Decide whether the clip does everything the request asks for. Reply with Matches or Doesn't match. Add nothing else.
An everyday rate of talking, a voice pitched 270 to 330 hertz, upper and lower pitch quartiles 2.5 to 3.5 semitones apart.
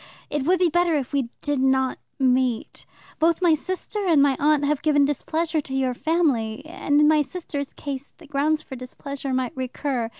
Matches